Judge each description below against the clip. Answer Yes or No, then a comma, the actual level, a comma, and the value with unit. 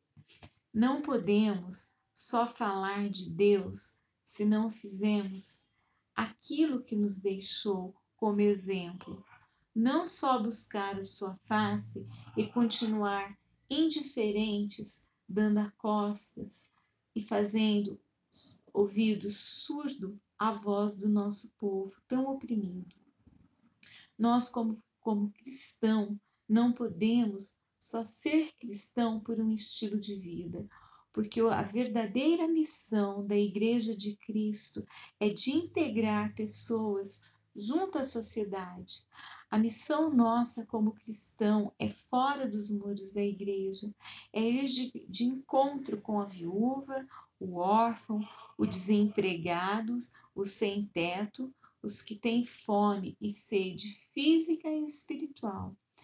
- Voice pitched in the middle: No, high, 215 Hz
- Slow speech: Yes, slow, 110 wpm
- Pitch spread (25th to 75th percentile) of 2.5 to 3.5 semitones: Yes, average, 2.8 semitones